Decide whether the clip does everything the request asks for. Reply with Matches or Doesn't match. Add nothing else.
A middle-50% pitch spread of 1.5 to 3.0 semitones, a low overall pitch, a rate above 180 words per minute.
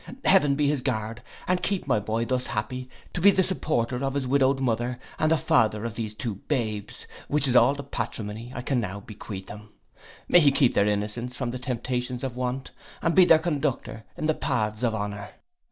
Doesn't match